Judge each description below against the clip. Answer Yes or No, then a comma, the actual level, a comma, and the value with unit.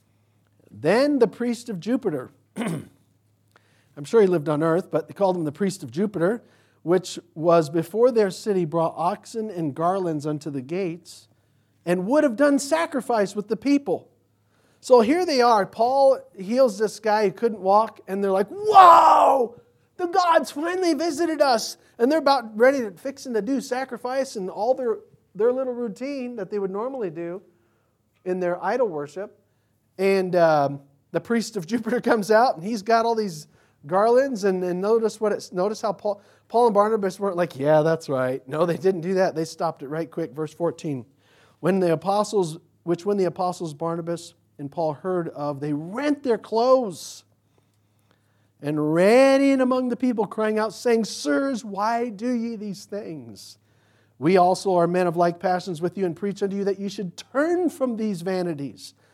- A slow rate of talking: No, average, 180 wpm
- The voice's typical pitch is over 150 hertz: Yes, high, 190 Hz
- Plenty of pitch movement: Yes, wide, 6.4 semitones